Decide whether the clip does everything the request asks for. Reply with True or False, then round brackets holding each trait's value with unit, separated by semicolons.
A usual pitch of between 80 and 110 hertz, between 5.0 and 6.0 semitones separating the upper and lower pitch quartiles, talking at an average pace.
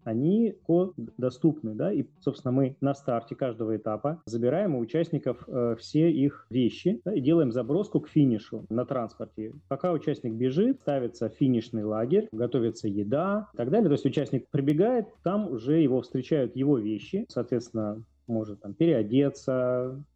False (130 Hz; 5.3 semitones; 150 wpm)